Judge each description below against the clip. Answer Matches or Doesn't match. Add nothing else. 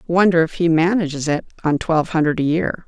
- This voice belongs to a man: Doesn't match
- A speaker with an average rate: Doesn't match